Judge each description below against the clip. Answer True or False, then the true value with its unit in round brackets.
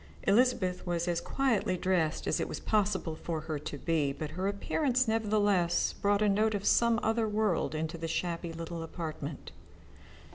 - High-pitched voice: False (180 Hz)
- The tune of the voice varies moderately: True (4.6 semitones)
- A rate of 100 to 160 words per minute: False (170 wpm)